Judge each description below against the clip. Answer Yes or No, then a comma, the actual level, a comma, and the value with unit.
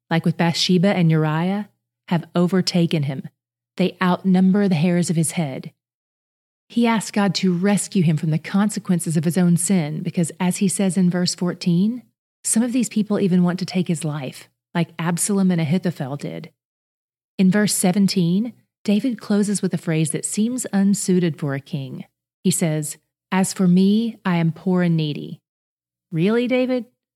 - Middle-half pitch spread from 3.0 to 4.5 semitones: Yes, average, 3.3 semitones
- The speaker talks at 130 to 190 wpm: Yes, average, 170 wpm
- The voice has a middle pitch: Yes, medium, 180 Hz